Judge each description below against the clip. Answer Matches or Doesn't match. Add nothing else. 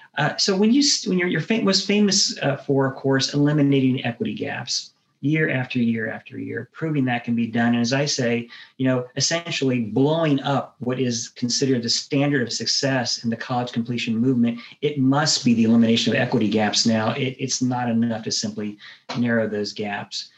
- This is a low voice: Matches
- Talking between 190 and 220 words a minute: Matches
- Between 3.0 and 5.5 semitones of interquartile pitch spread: Matches